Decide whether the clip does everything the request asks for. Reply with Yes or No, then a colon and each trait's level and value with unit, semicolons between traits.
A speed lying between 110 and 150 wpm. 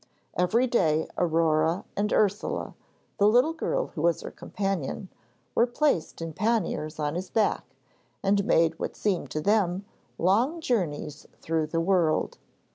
Yes: average, 140 wpm